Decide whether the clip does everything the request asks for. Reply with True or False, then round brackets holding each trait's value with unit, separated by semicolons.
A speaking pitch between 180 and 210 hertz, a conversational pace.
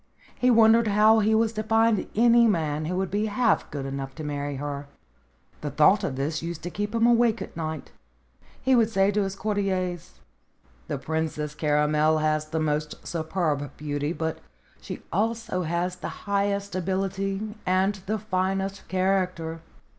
True (185 Hz; 160 wpm)